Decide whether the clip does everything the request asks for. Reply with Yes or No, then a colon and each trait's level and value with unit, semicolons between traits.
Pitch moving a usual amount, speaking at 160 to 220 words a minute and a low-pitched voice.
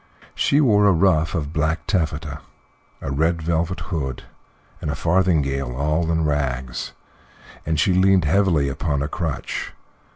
No: average, 3.3 semitones; average, 140 wpm; very low, 80 Hz